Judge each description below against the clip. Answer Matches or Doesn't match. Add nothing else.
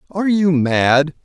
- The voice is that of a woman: Doesn't match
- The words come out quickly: Doesn't match